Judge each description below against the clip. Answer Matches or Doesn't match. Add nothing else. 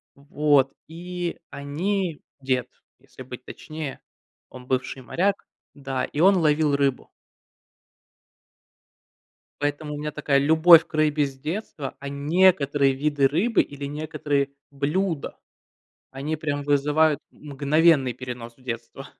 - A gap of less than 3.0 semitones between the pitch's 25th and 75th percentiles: Matches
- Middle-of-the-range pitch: Matches